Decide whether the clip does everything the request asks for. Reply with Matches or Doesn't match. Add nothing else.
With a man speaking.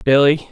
Matches